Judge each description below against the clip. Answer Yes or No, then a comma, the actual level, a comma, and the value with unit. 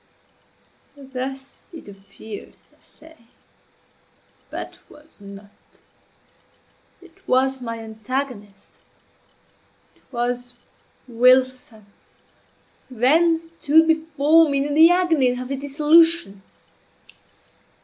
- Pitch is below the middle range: No, very high, 270 Hz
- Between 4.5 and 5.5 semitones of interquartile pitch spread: Yes, average, 4.8 semitones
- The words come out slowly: Yes, slow, 85 wpm